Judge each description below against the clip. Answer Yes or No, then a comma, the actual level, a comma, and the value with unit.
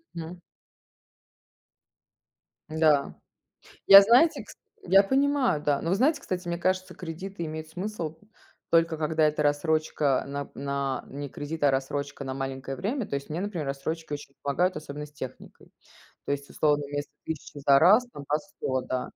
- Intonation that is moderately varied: Yes, average, 4.4 semitones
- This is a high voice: No, medium, 155 Hz